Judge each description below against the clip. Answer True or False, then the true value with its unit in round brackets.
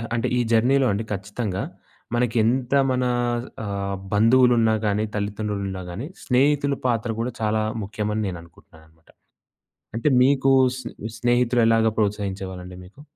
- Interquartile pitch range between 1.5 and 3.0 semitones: False (3.7 semitones)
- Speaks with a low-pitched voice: True (110 Hz)